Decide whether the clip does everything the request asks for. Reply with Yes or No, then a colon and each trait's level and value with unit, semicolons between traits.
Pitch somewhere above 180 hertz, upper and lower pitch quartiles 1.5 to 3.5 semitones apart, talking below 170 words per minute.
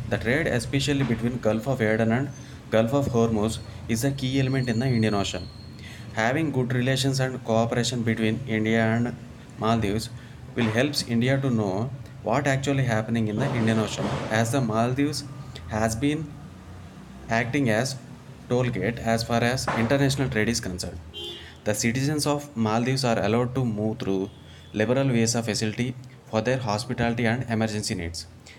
No: low, 115 Hz; average, 3.0 semitones; average, 155 wpm